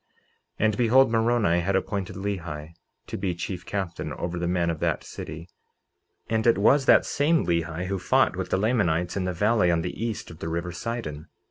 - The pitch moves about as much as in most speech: Yes, average, 4.6 semitones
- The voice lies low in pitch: Yes, very low, 95 Hz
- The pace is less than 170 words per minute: No, average, 200 wpm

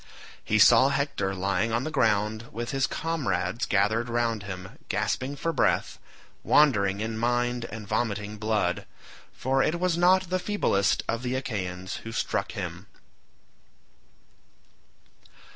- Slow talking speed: Yes, slow, 130 wpm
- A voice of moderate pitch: No, low, 115 Hz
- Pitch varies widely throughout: No, average, 4.7 semitones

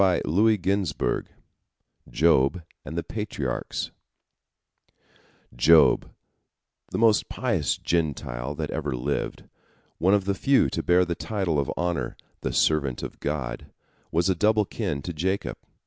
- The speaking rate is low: Yes, slow, 130 wpm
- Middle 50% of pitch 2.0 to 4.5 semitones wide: No, average, 4.9 semitones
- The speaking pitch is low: Yes, very low, 85 Hz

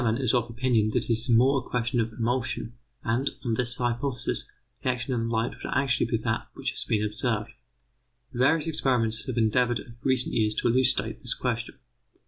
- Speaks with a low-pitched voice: Yes, low, 120 Hz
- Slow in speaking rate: No, average, 195 wpm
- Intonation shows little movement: Yes, narrow, 2.1 semitones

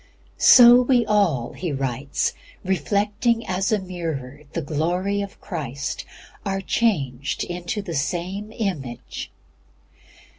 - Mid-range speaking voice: Yes, medium, 180 Hz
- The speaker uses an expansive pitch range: Yes, wide, 6.2 semitones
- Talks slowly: Yes, slow, 110 wpm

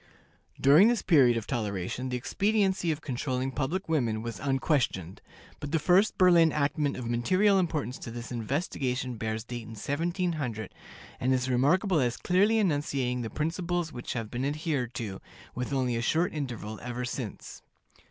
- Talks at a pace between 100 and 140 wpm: No, average, 160 wpm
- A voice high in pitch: No, low, 135 Hz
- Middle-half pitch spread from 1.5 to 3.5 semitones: No, wide, 5.4 semitones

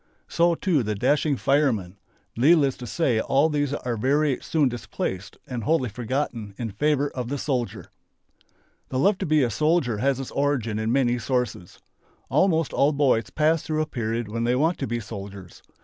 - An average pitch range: Yes, average, 4.5 semitones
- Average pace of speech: Yes, average, 180 wpm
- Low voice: Yes, low, 130 Hz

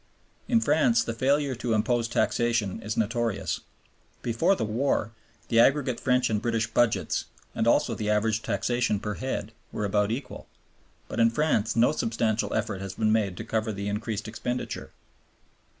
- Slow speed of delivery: No, average, 160 wpm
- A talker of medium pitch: No, low, 115 Hz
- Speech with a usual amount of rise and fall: No, narrow, 2.3 semitones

